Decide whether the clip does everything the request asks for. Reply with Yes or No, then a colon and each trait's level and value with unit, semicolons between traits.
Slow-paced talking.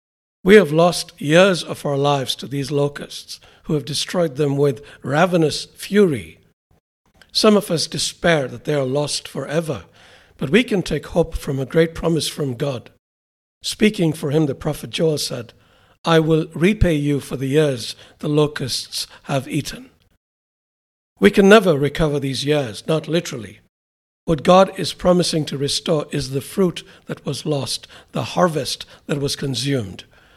No: average, 160 wpm